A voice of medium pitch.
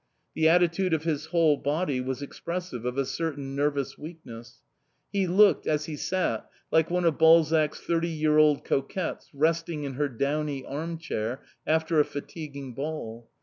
Yes: medium, 155 Hz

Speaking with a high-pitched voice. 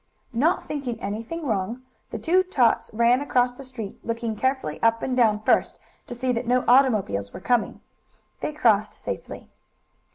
Yes: high, 240 Hz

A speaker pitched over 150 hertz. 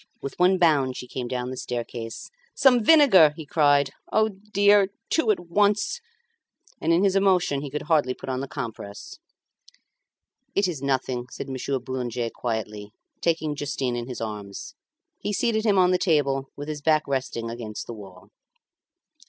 No: medium, 145 Hz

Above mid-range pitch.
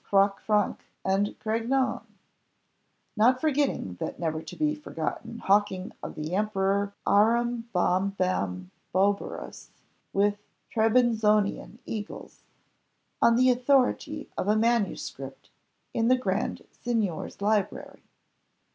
Yes: high, 210 Hz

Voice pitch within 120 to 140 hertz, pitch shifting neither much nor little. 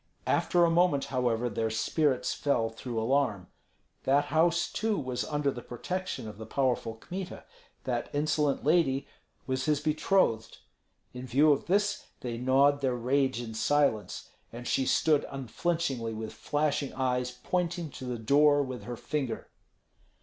Yes: low, 135 Hz; average, 3.8 semitones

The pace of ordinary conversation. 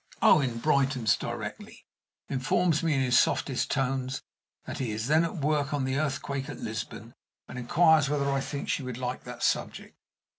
Yes: average, 175 wpm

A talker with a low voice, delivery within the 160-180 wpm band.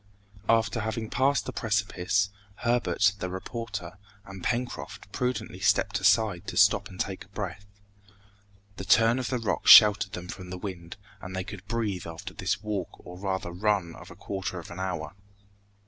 Yes: low, 100 Hz; average, 165 wpm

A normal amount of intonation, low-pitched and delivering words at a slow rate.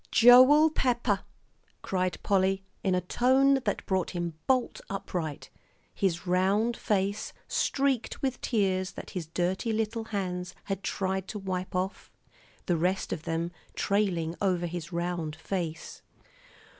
No: average, 3.7 semitones; high, 190 Hz; slow, 130 wpm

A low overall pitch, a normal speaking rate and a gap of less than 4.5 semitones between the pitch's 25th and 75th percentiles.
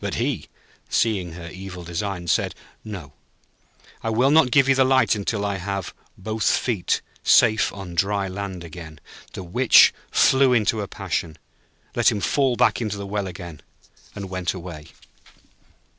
Yes: low, 100 Hz; average, 160 wpm; average, 3.9 semitones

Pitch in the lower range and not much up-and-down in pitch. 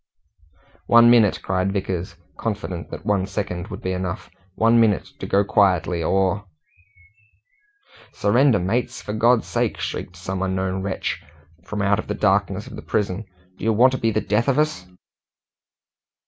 No: low, 100 Hz; average, 3.3 semitones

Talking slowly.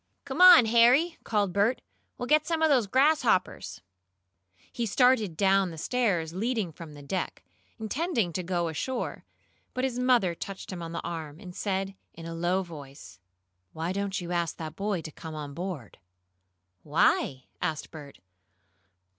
No: average, 160 wpm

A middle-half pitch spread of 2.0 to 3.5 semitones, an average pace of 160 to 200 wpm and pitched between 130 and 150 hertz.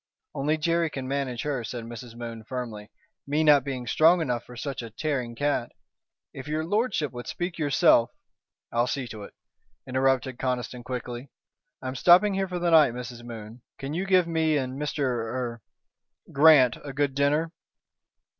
No: average, 4.2 semitones; average, 170 wpm; low, 135 Hz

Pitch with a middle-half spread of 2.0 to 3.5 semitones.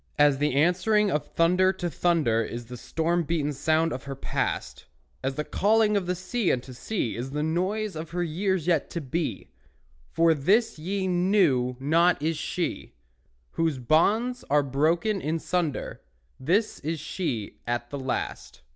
No: average, 4.6 semitones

